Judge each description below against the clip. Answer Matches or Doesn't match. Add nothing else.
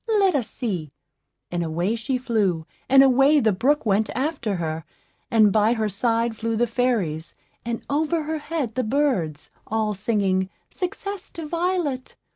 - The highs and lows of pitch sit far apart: Matches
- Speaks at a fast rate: Doesn't match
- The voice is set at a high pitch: Matches